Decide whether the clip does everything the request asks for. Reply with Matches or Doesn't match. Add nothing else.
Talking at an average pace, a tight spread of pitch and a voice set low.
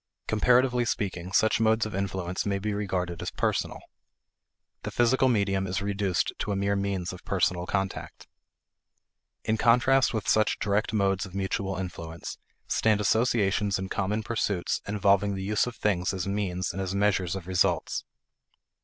Matches